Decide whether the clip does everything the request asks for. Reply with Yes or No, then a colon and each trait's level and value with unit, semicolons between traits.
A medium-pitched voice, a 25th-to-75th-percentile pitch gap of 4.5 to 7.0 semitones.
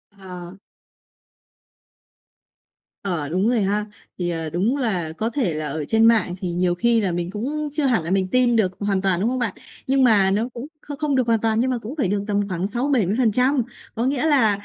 No: high, 210 Hz; average, 5.2 semitones